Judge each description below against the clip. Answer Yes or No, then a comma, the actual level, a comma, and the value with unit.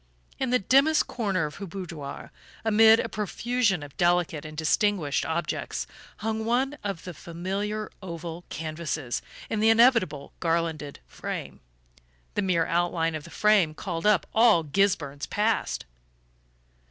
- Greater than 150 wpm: No, slow, 135 wpm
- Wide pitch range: No, average, 4.9 semitones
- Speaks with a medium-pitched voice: Yes, medium, 180 Hz